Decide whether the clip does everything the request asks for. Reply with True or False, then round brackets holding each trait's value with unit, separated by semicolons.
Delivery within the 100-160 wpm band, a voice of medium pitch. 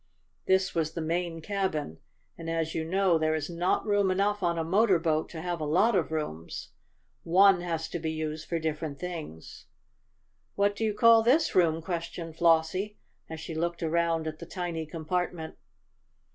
False (175 wpm; 170 Hz)